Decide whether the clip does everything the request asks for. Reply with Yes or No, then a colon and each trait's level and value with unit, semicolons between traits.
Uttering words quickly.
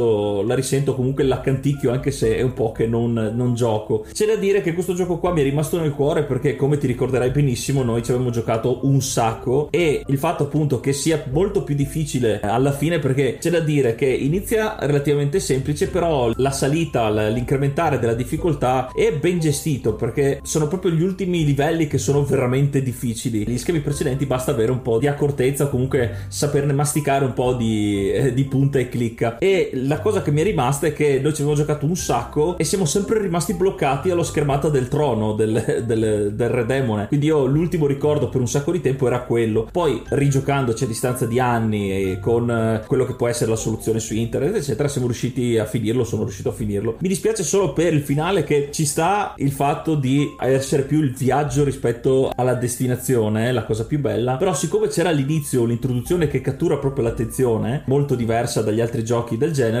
Yes: fast, 200 wpm